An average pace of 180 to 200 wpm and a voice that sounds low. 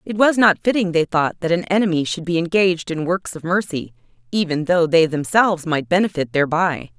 No: average, 195 wpm; medium, 170 Hz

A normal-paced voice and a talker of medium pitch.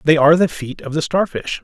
No: fast, 255 wpm; medium, 160 Hz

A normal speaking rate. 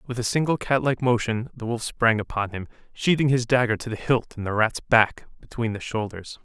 No: fast, 215 wpm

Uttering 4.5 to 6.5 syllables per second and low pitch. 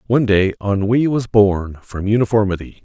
Yes: 5.2 syllables/s; low, 105 Hz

